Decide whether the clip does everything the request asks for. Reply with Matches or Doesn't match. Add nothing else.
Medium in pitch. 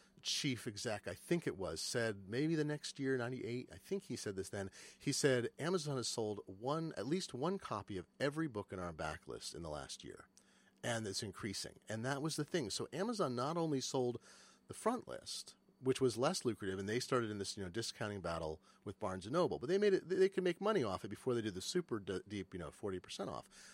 Doesn't match